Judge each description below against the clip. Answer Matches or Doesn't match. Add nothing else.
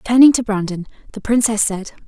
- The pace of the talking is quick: Doesn't match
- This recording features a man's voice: Doesn't match